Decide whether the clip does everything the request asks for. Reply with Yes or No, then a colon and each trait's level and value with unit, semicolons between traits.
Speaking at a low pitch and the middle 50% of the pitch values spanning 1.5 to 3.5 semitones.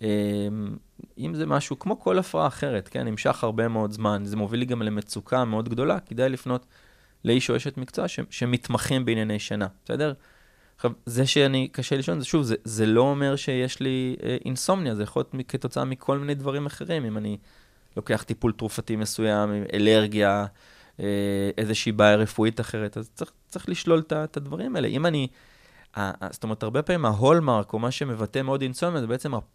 No: low, 120 Hz; average, 3.9 semitones